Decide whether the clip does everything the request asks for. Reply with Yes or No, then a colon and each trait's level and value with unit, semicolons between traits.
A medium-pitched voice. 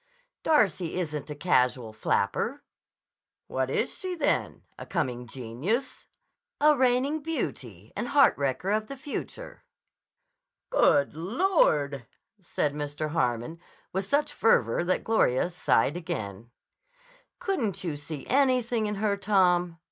Yes: medium, 180 Hz